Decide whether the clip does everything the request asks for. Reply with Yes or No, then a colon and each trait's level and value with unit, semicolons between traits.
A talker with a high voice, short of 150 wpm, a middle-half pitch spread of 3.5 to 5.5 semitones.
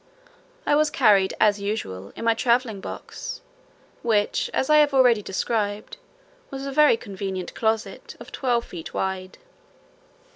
Yes: high, 220 Hz; average, 140 wpm; average, 4.8 semitones